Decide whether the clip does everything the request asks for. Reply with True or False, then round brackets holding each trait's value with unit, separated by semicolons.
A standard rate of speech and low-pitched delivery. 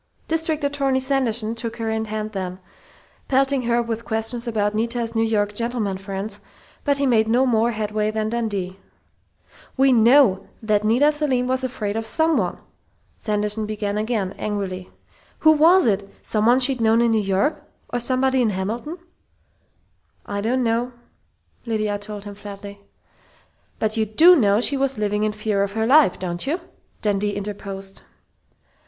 False (155 wpm; 220 Hz)